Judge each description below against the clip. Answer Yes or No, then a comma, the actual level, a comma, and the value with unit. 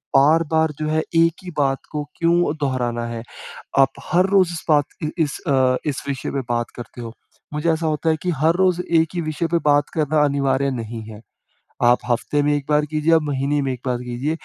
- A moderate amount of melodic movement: Yes, average, 3.3 semitones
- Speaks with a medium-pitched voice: Yes, medium, 145 Hz